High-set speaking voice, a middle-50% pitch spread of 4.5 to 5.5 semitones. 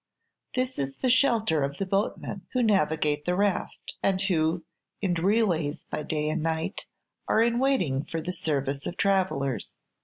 No: medium, 175 Hz; average, 5.2 semitones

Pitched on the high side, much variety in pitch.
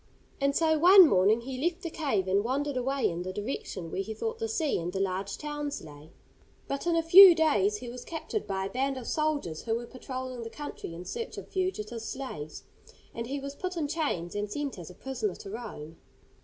Yes: very high, 255 Hz; wide, 7.5 semitones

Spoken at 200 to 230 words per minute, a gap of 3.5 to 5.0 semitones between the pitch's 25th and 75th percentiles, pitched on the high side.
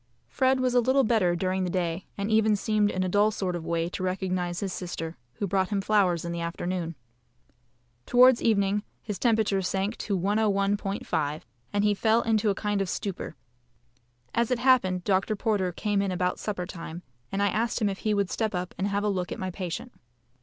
No: fast, 205 wpm; average, 2.9 semitones; high, 200 Hz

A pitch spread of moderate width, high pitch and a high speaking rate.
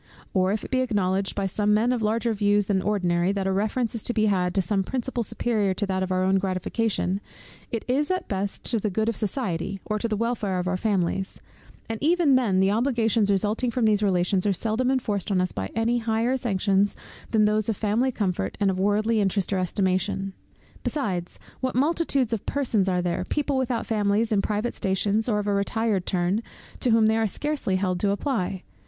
Yes: average, 3.2 semitones; high, 210 Hz; fast, 210 wpm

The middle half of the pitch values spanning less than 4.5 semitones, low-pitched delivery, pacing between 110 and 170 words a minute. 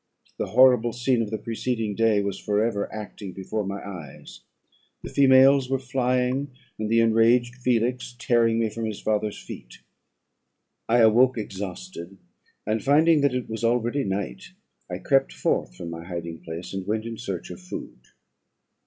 Yes: average, 3.9 semitones; low, 115 Hz; average, 160 wpm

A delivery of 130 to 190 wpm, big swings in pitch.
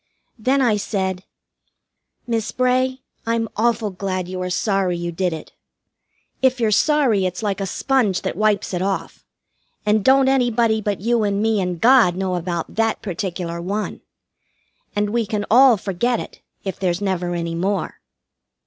No: average, 160 wpm; average, 4.0 semitones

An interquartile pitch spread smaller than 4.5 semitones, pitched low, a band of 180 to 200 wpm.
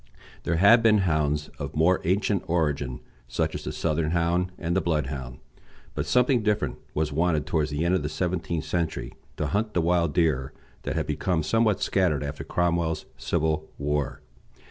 No: average, 3.4 semitones; very low, 85 Hz; average, 170 wpm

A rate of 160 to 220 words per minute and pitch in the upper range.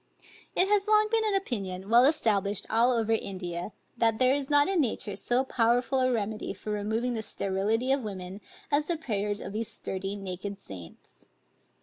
Yes: average, 180 wpm; high, 225 Hz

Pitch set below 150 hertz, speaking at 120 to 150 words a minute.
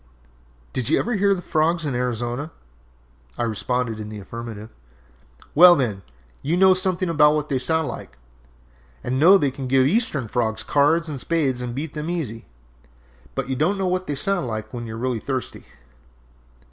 No: medium, 140 Hz; average, 180 wpm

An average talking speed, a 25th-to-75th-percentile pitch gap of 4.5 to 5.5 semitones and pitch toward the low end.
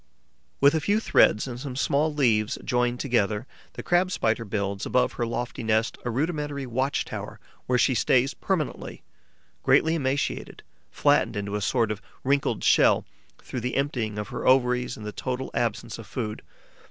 No: average, 165 wpm; average, 4.0 semitones; low, 125 Hz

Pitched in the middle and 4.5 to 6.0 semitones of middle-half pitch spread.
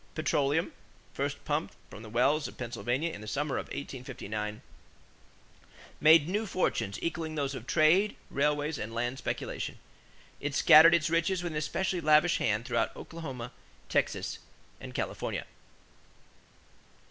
Yes: medium, 150 Hz; average, 5.1 semitones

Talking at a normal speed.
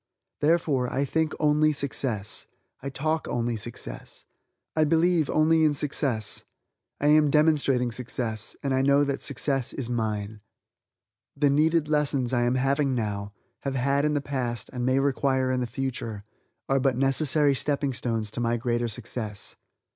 Yes: average, 155 wpm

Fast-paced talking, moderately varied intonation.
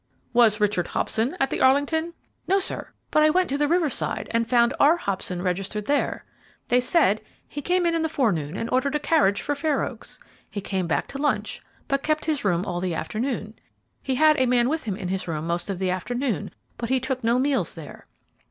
No: fast, 215 wpm; wide, 6.8 semitones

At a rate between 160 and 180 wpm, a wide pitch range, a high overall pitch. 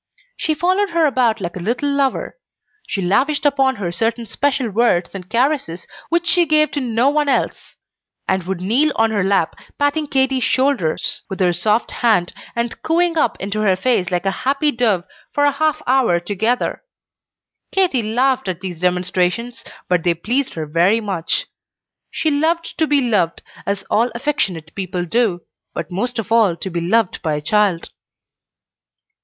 Yes: average, 170 wpm; wide, 7.2 semitones; high, 230 Hz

